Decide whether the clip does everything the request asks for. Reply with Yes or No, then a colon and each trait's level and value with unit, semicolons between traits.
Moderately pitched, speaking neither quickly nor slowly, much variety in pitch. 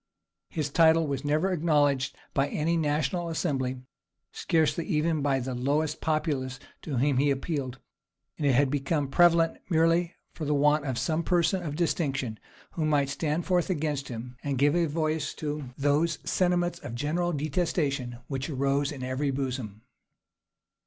No: medium, 145 Hz; average, 150 wpm; average, 3.2 semitones